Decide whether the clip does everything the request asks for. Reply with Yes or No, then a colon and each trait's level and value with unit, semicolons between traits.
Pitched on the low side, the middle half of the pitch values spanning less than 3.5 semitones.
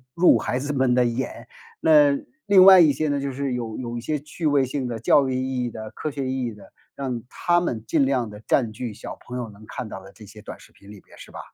No: low, 130 Hz; average, 3.8 semitones